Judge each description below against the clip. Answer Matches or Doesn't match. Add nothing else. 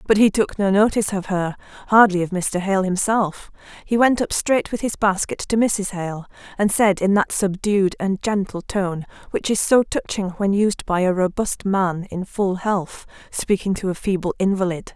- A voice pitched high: Matches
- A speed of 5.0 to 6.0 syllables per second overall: Doesn't match